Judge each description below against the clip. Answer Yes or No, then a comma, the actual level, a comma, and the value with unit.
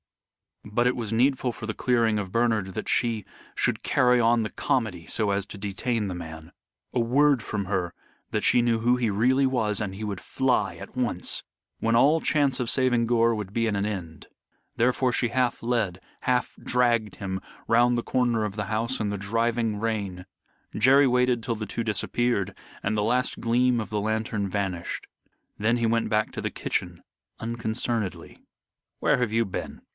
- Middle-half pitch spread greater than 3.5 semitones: No, average, 2.9 semitones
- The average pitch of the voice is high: No, low, 115 Hz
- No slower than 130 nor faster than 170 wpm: No, average, 185 wpm